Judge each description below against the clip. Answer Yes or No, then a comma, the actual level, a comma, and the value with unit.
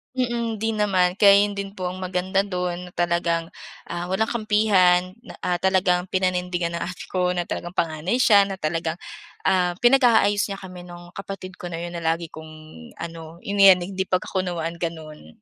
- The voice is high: No, medium, 180 Hz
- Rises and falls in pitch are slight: Yes, narrow, 2.3 semitones